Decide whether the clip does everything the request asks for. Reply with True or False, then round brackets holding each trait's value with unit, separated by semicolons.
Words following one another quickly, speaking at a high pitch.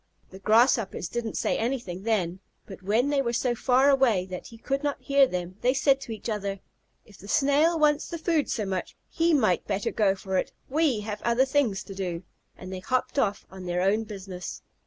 True (210 wpm; 220 Hz)